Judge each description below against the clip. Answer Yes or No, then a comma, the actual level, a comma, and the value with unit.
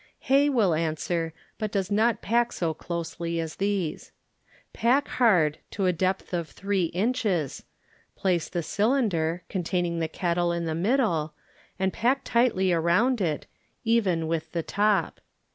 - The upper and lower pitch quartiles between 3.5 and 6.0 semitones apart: Yes, average, 4.6 semitones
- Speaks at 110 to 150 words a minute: Yes, average, 145 wpm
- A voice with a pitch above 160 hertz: Yes, medium, 185 Hz